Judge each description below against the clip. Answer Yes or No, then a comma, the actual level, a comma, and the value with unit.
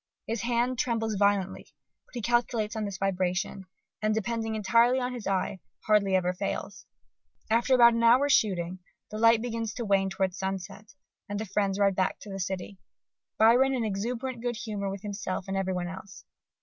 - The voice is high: Yes, high, 210 Hz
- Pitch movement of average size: Yes, average, 3.2 semitones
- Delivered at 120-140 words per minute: No, average, 175 wpm